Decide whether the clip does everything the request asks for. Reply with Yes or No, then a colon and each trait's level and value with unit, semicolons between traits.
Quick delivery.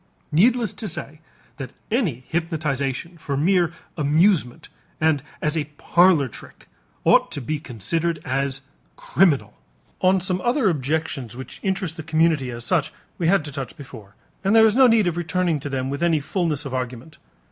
No: average, 170 wpm